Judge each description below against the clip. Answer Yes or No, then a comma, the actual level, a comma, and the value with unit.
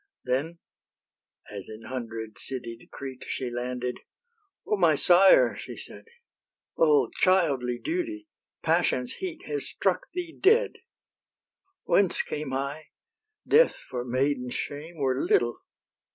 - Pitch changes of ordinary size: No, wide, 7.7 semitones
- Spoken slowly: Yes, slow, 115 wpm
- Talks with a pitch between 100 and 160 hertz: Yes, medium, 140 Hz